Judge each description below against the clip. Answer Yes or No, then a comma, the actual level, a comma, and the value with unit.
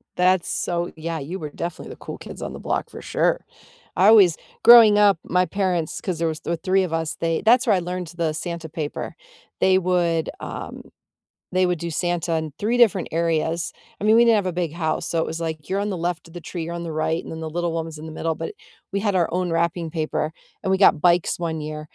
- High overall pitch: No, medium, 170 Hz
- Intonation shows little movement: Yes, narrow, 2.3 semitones